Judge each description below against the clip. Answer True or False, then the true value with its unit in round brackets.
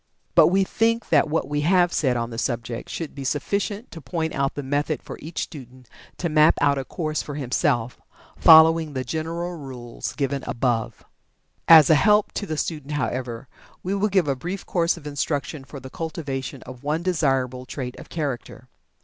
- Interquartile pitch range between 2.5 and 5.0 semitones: True (4.1 semitones)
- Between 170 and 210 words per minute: True (185 wpm)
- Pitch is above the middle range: False (145 Hz)